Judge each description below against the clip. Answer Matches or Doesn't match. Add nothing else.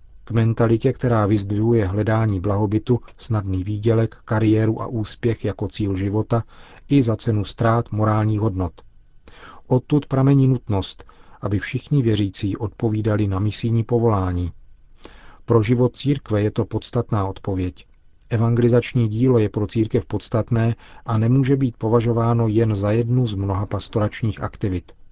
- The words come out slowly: Doesn't match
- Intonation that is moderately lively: Doesn't match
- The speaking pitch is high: Doesn't match